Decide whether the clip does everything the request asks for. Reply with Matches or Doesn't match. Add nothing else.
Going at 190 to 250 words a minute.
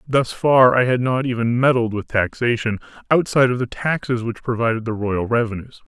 Doesn't match